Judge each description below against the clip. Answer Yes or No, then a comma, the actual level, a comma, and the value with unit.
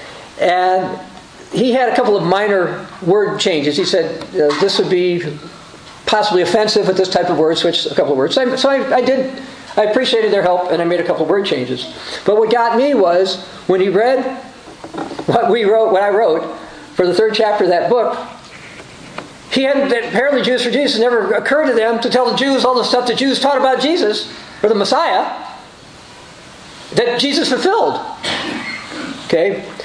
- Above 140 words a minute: Yes, average, 190 wpm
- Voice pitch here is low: No, high, 230 Hz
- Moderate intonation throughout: No, wide, 5.8 semitones